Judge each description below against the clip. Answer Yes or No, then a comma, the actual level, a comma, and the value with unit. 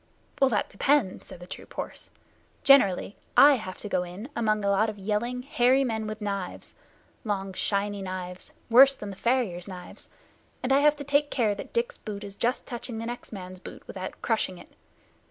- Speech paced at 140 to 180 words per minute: No, average, 190 wpm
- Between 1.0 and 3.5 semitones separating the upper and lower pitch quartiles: No, average, 4.5 semitones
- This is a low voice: No, high, 215 Hz